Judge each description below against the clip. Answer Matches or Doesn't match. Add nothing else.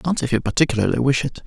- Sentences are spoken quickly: Matches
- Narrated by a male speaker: Matches